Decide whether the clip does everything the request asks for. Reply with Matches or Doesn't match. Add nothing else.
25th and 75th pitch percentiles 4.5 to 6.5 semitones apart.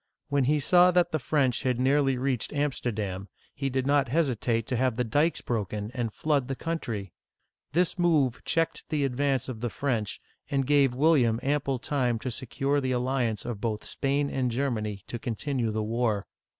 Doesn't match